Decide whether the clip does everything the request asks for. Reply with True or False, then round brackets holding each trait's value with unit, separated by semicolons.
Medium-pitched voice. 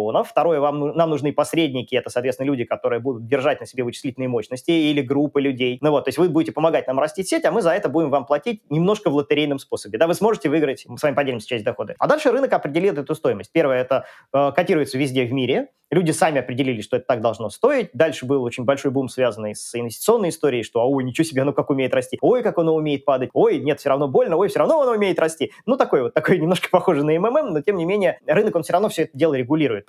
True (150 Hz)